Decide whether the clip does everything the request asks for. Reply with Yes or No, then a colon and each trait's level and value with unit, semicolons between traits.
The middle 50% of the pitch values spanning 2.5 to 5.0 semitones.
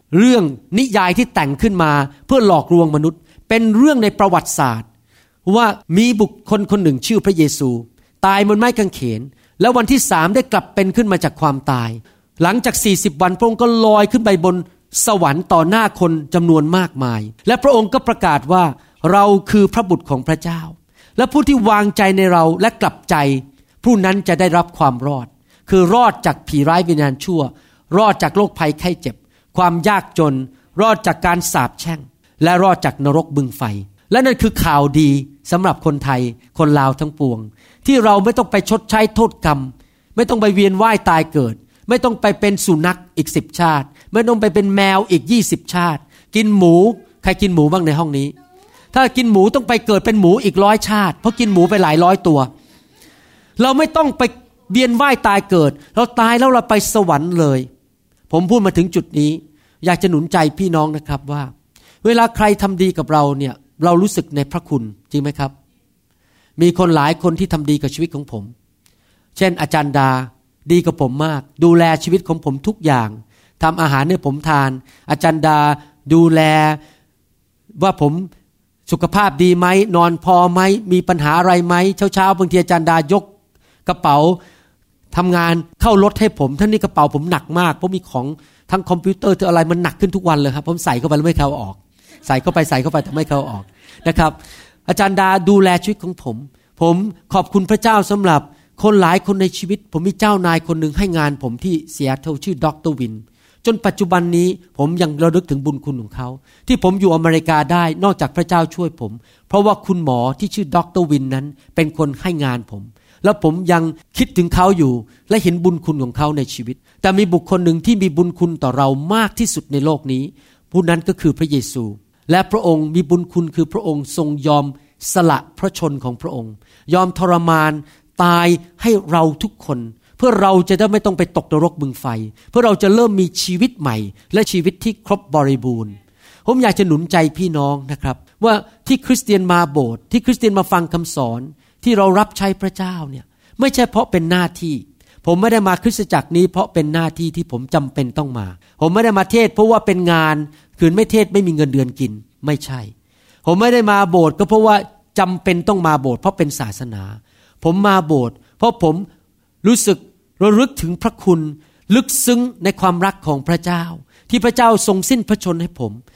No: wide, 5.4 semitones